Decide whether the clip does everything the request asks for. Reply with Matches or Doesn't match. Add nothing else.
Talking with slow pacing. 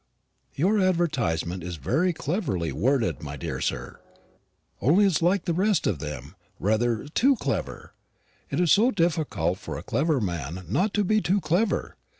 Doesn't match